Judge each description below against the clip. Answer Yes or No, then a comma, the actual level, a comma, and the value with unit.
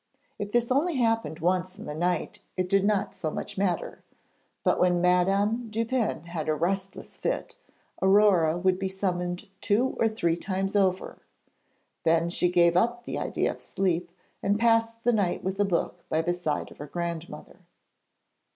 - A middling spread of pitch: Yes, average, 3.4 semitones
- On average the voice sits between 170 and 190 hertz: Yes, medium, 185 Hz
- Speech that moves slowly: No, average, 170 wpm